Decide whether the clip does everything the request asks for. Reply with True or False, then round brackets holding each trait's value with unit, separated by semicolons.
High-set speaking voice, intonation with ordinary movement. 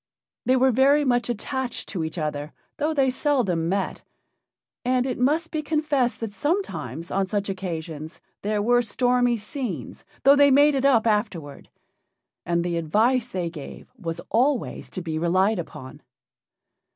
False (225 Hz; 7.3 semitones)